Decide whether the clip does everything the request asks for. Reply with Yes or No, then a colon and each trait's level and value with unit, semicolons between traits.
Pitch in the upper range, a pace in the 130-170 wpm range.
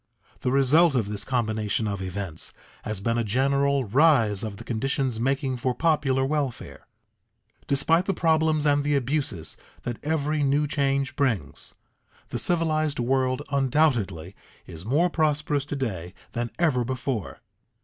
No: low, 135 Hz; average, 140 wpm